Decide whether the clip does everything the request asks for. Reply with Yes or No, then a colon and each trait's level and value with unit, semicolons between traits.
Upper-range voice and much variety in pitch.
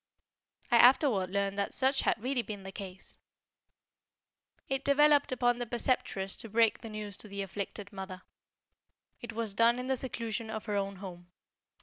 No: high, 220 Hz; average, 3.7 semitones